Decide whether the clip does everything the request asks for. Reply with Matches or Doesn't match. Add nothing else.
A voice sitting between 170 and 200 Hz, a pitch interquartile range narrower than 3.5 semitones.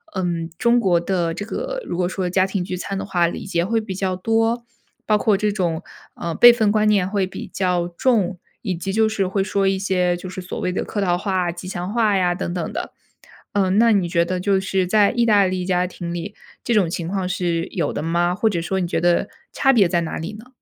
Matches